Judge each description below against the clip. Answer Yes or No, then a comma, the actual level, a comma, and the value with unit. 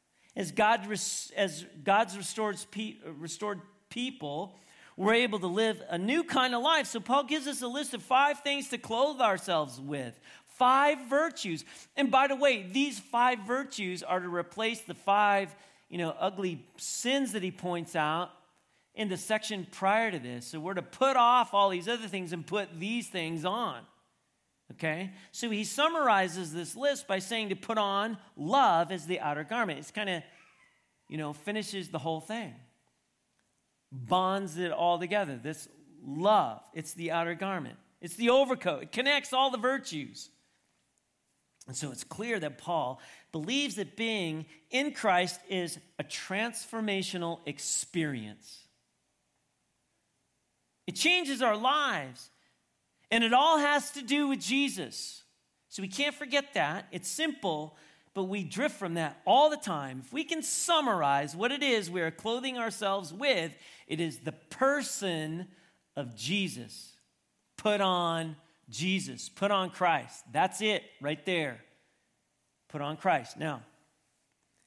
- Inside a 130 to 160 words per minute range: Yes, average, 150 wpm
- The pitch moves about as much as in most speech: No, wide, 6.4 semitones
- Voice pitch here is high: Yes, high, 195 Hz